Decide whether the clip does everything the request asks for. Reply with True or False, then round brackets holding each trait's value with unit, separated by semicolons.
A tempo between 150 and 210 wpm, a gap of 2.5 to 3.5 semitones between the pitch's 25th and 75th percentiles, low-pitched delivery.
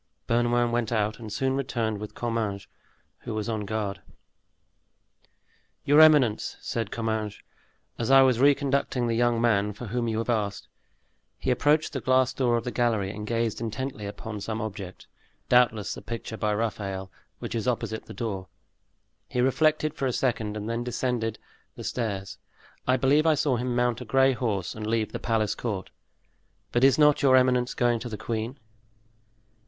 True (175 wpm; 2.9 semitones; 115 Hz)